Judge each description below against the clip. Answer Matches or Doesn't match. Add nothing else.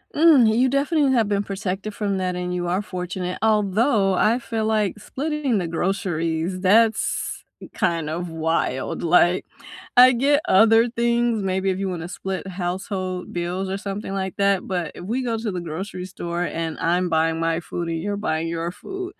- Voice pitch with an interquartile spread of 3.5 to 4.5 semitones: Matches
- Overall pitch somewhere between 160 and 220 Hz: Matches